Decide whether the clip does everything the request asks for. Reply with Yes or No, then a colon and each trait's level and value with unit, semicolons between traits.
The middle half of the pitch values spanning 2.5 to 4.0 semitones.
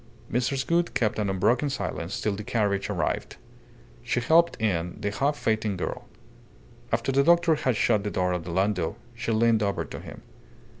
No: average, 4.8 semitones